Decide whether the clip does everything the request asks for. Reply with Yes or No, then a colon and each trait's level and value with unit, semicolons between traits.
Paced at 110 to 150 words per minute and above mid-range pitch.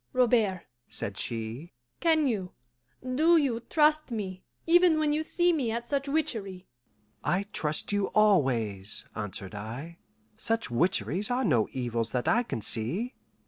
Yes: average, 145 wpm; high, 200 Hz